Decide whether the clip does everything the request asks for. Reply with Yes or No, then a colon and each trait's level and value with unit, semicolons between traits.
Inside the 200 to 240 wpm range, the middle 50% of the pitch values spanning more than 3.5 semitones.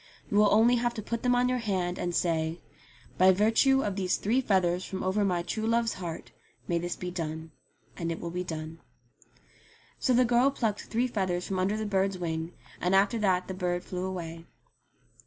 Yes: fast, 205 wpm; average, 4.0 semitones